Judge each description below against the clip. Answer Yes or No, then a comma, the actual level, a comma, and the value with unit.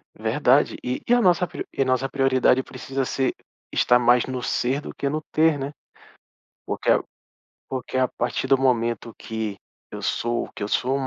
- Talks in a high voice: No, low, 130 Hz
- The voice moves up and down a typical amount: No, narrow, 2.0 semitones